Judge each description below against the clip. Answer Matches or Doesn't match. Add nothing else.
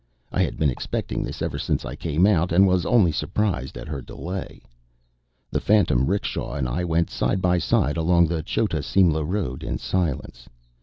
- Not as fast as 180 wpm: Doesn't match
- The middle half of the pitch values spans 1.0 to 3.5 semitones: Doesn't match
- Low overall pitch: Matches